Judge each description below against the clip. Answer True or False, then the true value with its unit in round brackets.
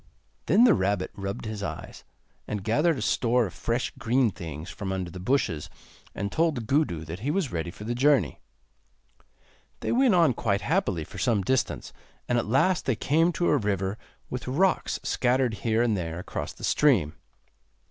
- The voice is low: True (115 Hz)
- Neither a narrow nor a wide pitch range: False (6.5 semitones)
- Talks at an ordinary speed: True (180 wpm)